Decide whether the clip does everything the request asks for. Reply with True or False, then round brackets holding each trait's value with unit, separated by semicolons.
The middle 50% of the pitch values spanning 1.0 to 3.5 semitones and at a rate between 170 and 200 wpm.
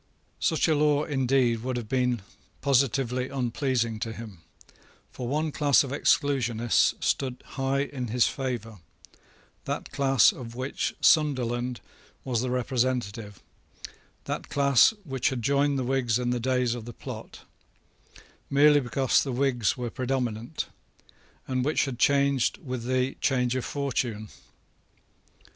False (2.4 semitones; 135 wpm)